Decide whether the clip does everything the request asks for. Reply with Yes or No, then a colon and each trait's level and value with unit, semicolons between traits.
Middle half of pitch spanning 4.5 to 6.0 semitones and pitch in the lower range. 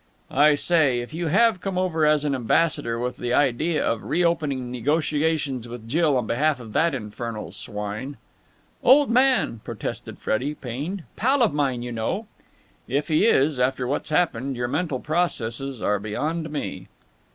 No: average, 5.1 semitones; medium, 145 Hz